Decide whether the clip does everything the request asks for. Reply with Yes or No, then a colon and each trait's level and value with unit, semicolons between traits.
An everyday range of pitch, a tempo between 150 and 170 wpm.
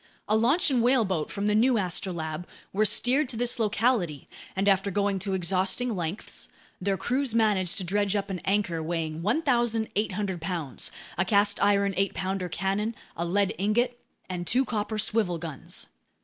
Yes: average, 3.4 semitones; average, 165 wpm